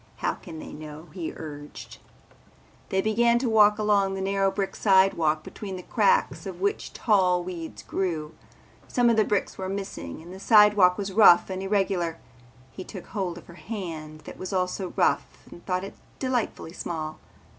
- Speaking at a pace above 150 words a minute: Yes, average, 175 wpm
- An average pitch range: Yes, average, 3.3 semitones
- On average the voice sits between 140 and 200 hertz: Yes, high, 190 Hz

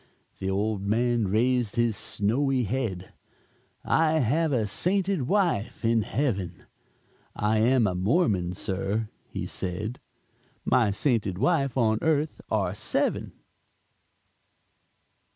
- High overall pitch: No, low, 115 Hz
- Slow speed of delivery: Yes, slow, 110 wpm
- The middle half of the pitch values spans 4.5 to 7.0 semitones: Yes, average, 5.1 semitones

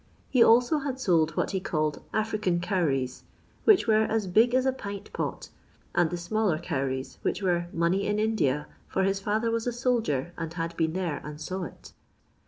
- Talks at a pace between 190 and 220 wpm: Yes, average, 195 wpm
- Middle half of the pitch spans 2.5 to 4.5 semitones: No, average, 5.2 semitones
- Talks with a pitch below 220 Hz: Yes, high, 190 Hz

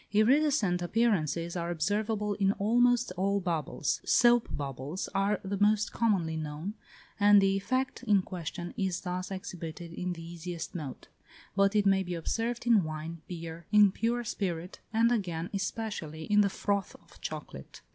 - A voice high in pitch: Yes, high, 195 Hz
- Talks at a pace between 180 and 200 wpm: No, average, 155 wpm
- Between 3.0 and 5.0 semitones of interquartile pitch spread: Yes, average, 3.9 semitones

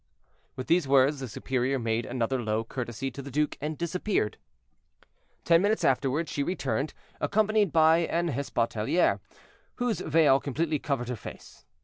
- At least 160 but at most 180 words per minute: No, average, 145 wpm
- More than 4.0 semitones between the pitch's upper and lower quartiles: Yes, average, 4.9 semitones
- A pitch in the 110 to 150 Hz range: Yes, medium, 140 Hz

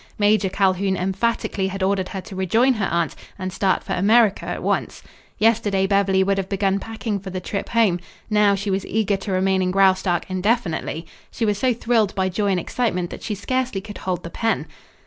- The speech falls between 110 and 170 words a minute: No, average, 200 wpm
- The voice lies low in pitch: No, high, 195 Hz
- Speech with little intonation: Yes, narrow, 2.2 semitones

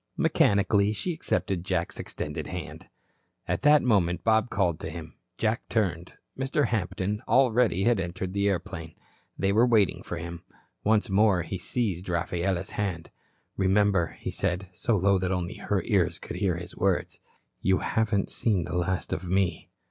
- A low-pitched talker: Yes, very low, 95 Hz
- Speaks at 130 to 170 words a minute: Yes, average, 160 wpm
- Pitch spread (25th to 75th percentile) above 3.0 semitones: Yes, average, 3.4 semitones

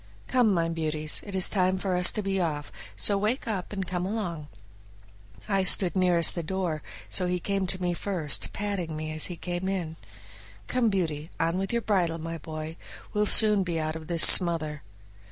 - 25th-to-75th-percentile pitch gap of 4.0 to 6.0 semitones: No, average, 3.2 semitones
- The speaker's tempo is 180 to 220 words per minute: Yes, average, 190 wpm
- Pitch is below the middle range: No, medium, 180 Hz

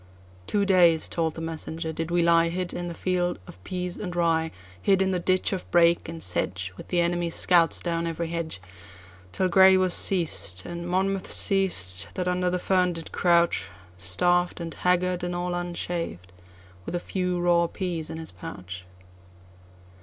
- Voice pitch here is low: No, medium, 170 Hz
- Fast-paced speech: No, average, 160 wpm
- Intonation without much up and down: Yes, narrow, 2.0 semitones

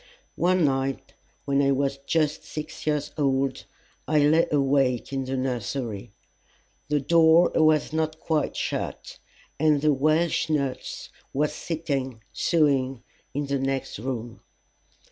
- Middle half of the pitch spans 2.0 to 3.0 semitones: Yes, narrow, 2.6 semitones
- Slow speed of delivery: Yes, slow, 125 wpm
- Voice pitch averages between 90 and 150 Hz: Yes, medium, 140 Hz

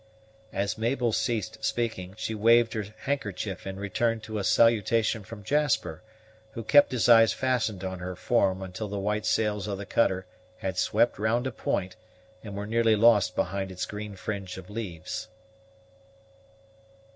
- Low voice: Yes, low, 105 Hz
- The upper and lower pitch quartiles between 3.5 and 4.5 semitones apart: No, average, 3.1 semitones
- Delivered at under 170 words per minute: Yes, average, 155 wpm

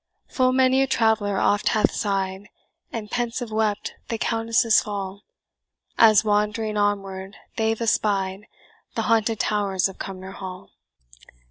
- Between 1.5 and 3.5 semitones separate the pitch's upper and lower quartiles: Yes, narrow, 2.4 semitones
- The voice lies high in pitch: Yes, high, 210 Hz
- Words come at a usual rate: No, slow, 125 wpm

